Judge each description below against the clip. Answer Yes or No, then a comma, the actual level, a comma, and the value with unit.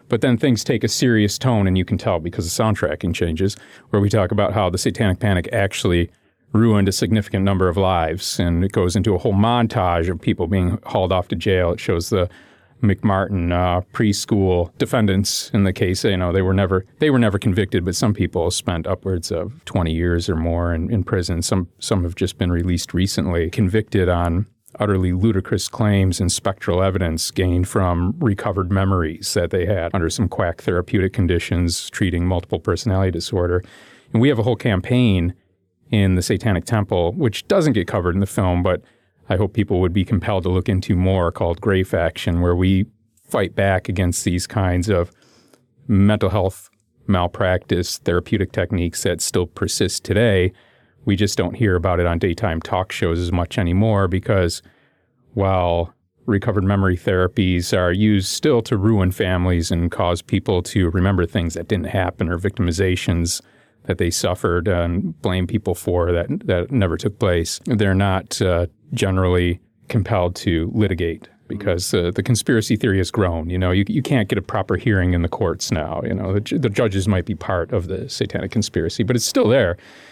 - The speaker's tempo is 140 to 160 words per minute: No, average, 185 wpm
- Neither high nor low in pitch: No, very low, 95 Hz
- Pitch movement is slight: No, average, 3.1 semitones